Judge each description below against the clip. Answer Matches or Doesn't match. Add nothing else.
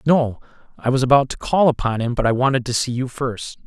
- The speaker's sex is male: Matches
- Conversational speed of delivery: Doesn't match